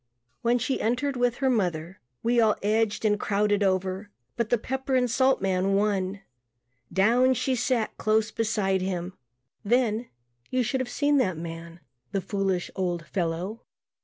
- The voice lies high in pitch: Yes, high, 210 Hz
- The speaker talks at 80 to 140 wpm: No, average, 155 wpm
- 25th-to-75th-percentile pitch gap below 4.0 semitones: No, average, 4.4 semitones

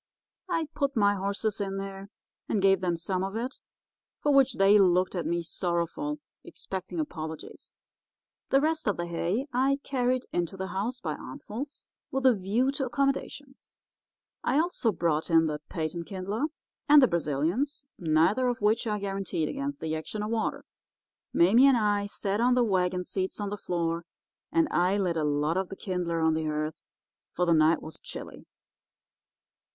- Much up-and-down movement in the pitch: Yes, wide, 6.3 semitones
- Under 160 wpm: No, average, 170 wpm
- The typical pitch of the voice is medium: No, high, 195 Hz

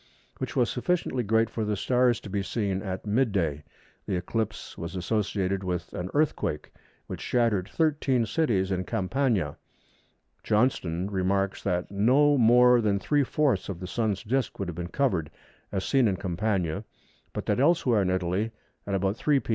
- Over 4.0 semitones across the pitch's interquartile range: Yes, average, 4.9 semitones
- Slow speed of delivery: No, average, 170 wpm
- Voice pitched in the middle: No, low, 105 Hz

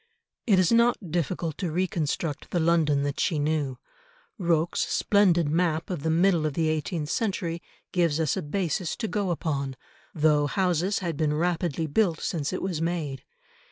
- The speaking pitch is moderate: Yes, medium, 165 Hz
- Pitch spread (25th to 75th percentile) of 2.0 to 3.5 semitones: Yes, average, 3.0 semitones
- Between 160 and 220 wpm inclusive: Yes, average, 165 wpm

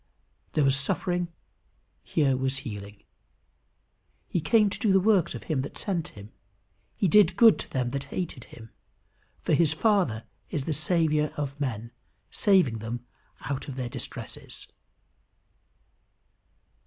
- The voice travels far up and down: Yes, wide, 6.2 semitones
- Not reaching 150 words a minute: Yes, average, 140 wpm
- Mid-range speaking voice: Yes, medium, 145 Hz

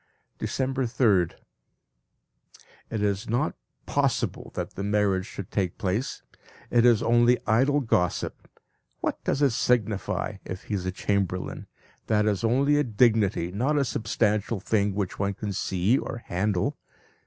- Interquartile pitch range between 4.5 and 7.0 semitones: No, average, 3.4 semitones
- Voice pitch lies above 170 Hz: No, low, 105 Hz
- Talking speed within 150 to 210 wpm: No, average, 140 wpm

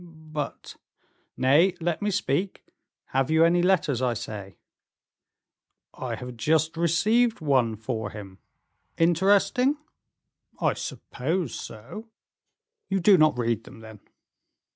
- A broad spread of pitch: Yes, wide, 7.3 semitones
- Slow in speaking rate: Yes, slow, 120 wpm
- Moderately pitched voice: Yes, medium, 155 Hz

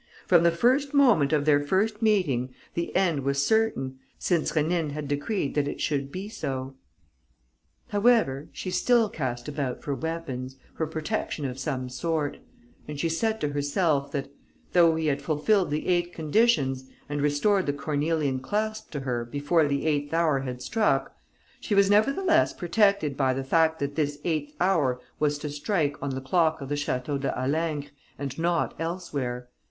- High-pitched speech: No, medium, 150 Hz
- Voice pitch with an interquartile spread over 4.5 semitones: No, average, 4.1 semitones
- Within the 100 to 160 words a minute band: No, average, 170 wpm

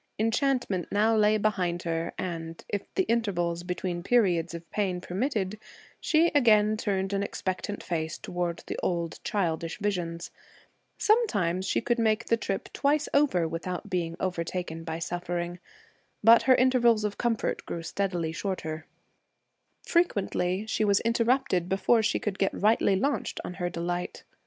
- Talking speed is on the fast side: No, average, 145 wpm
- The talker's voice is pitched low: No, high, 190 Hz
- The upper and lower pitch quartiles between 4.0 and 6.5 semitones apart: Yes, average, 4.4 semitones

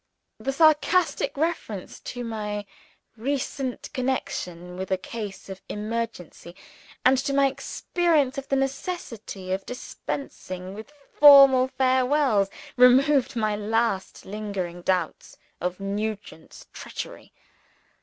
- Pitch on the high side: Yes, high, 230 Hz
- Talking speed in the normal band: No, slow, 105 wpm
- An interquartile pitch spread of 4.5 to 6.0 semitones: Yes, wide, 5.6 semitones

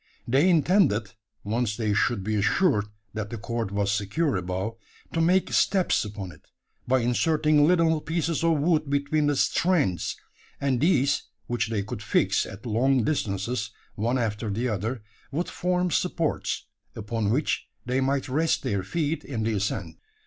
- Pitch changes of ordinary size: No, wide, 6.7 semitones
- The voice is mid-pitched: No, low, 125 Hz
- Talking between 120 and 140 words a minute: No, average, 155 wpm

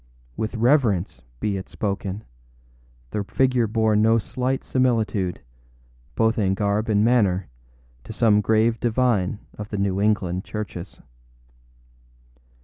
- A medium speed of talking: No, slow, 120 wpm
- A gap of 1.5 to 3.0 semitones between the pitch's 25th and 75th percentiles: Yes, narrow, 2.5 semitones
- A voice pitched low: Yes, low, 105 Hz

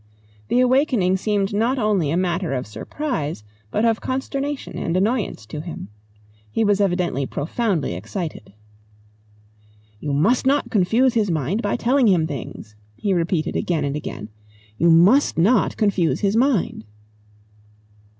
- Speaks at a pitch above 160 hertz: Yes, high, 190 Hz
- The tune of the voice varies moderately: No, wide, 6.6 semitones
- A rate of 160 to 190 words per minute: No, average, 140 wpm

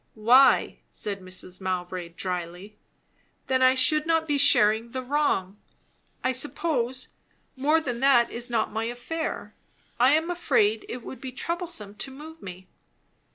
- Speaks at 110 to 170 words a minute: Yes, average, 145 wpm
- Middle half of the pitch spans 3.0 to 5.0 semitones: No, wide, 5.6 semitones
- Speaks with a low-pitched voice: No, high, 245 Hz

